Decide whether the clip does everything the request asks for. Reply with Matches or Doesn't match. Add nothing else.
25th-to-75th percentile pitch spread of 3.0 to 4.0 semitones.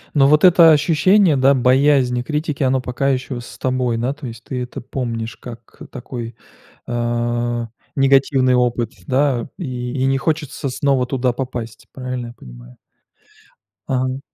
Doesn't match